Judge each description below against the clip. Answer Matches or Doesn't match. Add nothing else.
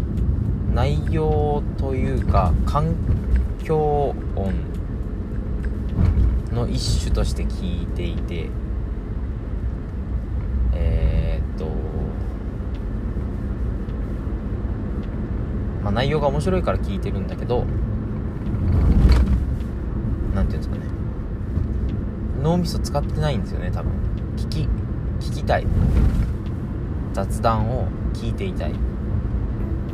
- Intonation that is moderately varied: Matches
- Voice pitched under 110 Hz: Matches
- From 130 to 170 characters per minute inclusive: Matches